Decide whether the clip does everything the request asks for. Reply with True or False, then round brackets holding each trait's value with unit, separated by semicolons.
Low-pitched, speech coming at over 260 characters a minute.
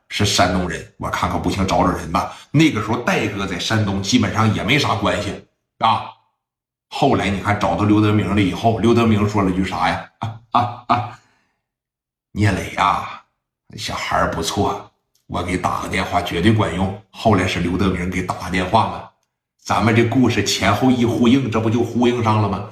True (105 Hz; 275 characters per minute)